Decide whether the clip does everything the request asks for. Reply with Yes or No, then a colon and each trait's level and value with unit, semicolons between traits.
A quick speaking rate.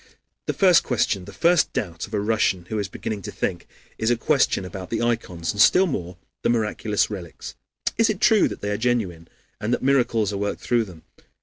Yes: fast, 210 wpm